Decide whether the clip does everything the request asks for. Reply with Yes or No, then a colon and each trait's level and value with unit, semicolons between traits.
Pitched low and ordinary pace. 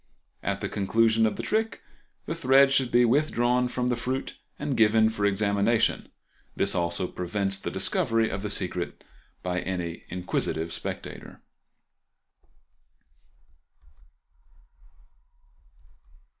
No: low, 110 Hz; slow, 110 wpm